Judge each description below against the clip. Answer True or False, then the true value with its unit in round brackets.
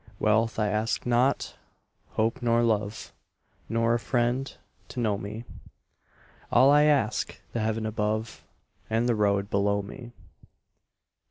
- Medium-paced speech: False (125 wpm)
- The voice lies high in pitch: False (115 Hz)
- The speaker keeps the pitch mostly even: True (2.0 semitones)